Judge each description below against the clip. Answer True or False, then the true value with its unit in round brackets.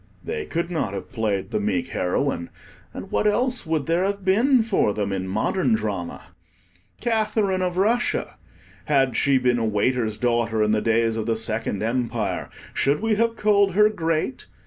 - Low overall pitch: True (130 Hz)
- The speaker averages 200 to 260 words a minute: False (170 wpm)